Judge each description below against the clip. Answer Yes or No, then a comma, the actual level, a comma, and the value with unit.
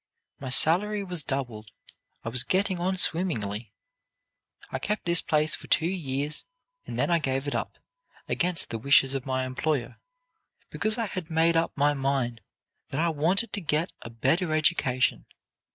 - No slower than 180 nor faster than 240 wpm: No, average, 165 wpm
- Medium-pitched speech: Yes, medium, 150 Hz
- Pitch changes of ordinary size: Yes, average, 4.9 semitones